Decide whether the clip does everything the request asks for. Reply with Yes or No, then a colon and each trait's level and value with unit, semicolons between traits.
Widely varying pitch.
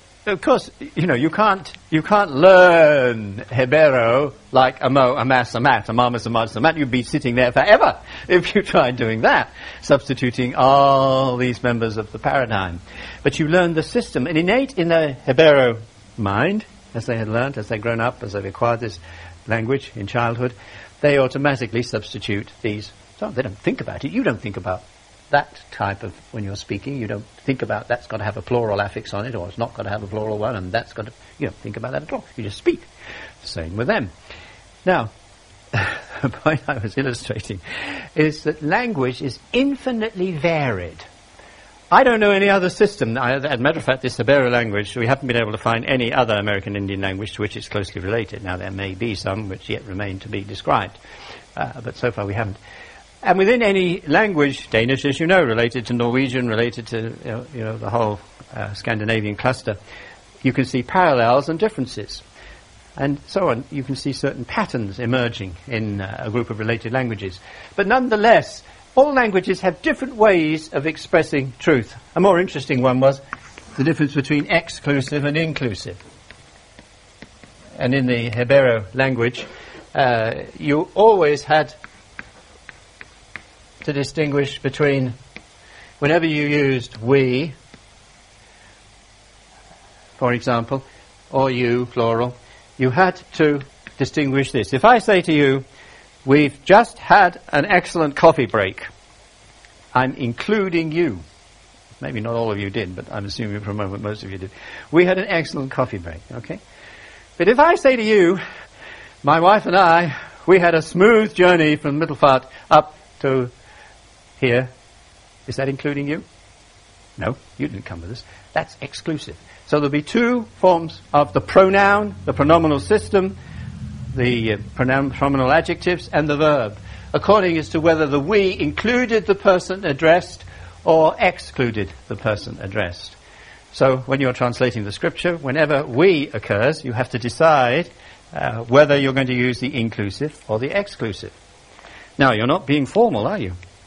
Yes: wide, 6.0 semitones